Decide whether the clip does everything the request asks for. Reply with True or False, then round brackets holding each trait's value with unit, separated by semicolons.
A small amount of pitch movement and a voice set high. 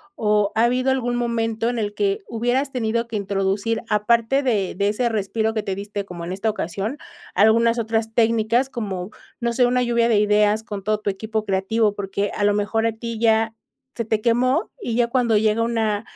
True (2.2 semitones; 225 Hz)